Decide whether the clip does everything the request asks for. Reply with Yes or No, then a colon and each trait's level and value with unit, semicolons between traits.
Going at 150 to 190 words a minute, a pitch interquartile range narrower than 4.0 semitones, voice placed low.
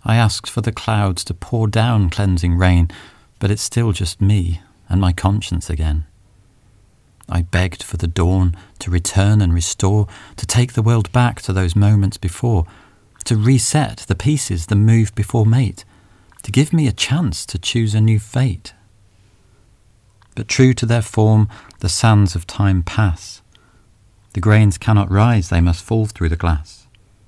Yes: average, 165 wpm; average, 3.2 semitones; low, 105 Hz